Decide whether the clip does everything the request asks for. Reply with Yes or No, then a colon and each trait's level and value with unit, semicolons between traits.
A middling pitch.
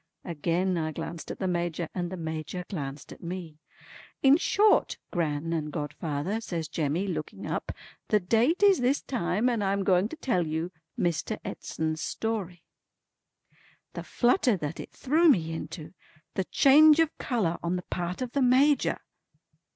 Yes: medium, 180 Hz